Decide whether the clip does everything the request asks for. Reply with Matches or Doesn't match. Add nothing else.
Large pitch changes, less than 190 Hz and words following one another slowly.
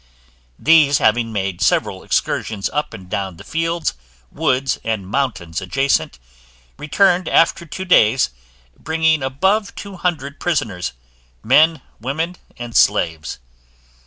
Matches